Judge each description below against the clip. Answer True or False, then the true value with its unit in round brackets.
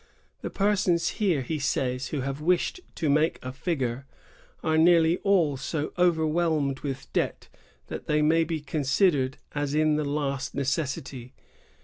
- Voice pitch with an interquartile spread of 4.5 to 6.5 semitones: False (3.2 semitones)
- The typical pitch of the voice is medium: True (150 Hz)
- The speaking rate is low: False (150 wpm)